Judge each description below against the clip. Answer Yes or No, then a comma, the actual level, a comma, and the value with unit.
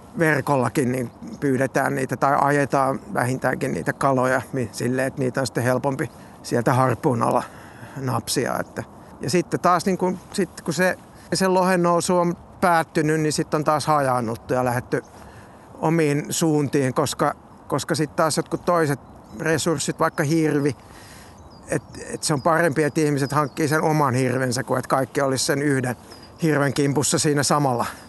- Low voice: No, medium, 145 Hz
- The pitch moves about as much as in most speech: Yes, average, 3.9 semitones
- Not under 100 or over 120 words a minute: No, fast, 155 wpm